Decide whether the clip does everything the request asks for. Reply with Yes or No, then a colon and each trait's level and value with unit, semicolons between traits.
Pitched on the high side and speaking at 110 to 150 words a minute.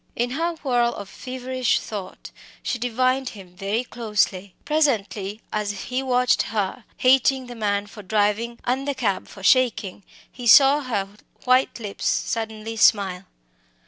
Yes: high, 235 Hz; average, 145 wpm